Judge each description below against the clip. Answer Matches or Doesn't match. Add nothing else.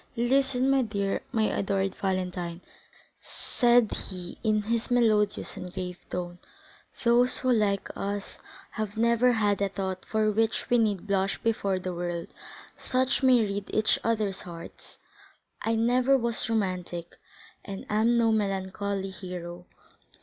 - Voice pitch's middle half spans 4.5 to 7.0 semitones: Doesn't match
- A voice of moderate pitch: Doesn't match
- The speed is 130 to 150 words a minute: Matches